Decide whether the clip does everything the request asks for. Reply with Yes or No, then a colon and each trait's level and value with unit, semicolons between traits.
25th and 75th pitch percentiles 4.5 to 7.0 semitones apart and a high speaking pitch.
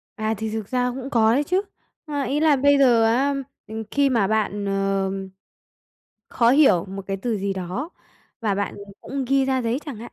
Yes: average, 5.1 semitones; high, 230 Hz